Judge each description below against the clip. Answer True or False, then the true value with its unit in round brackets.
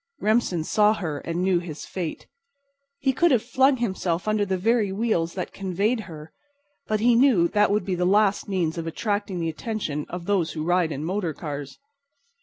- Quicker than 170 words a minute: True (190 wpm)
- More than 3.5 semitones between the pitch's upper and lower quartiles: True (4.3 semitones)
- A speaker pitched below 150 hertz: False (190 Hz)